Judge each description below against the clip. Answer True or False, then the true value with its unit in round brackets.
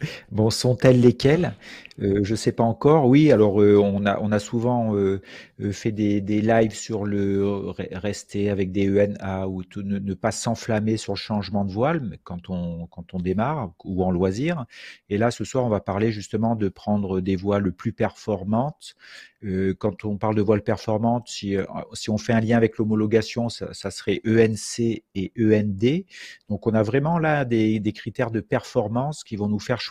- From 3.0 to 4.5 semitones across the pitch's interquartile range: False (2.6 semitones)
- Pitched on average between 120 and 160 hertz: False (105 Hz)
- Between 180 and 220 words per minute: True (200 wpm)